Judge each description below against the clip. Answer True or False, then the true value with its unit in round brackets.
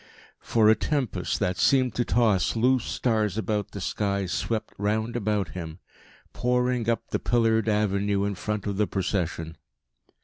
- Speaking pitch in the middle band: False (105 Hz)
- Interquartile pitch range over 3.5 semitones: False (2.8 semitones)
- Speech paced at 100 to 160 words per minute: True (150 wpm)